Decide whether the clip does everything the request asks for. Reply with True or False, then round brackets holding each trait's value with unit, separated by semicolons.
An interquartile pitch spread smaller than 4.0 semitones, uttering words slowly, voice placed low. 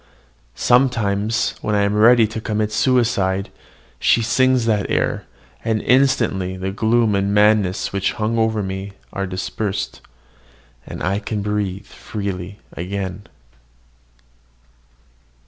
True (2.4 semitones; 110 wpm; 105 Hz)